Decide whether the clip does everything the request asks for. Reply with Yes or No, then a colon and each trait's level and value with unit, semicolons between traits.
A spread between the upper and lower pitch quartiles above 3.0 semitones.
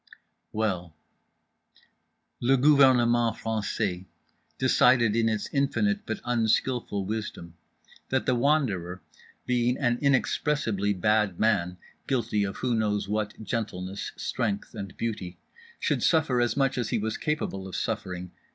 Yes: average, 3.9 semitones